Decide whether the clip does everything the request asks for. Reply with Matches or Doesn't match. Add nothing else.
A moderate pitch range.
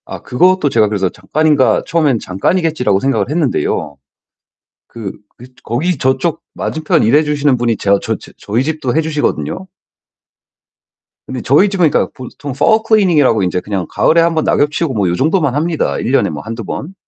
Doesn't match